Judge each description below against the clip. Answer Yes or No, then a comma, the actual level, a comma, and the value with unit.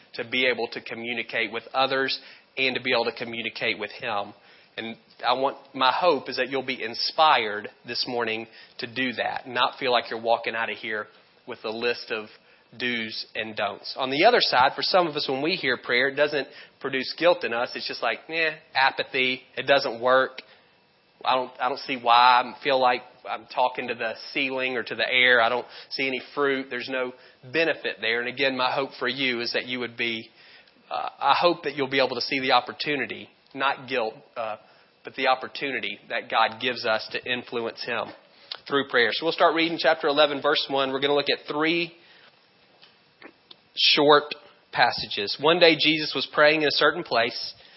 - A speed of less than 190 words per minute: No, average, 200 wpm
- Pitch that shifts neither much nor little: Yes, average, 3.0 semitones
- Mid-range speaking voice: No, low, 130 Hz